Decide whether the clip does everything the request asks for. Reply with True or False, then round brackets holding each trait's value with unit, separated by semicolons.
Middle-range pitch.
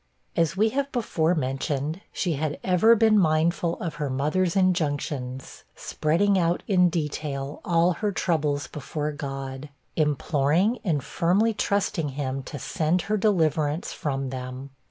True (155 Hz)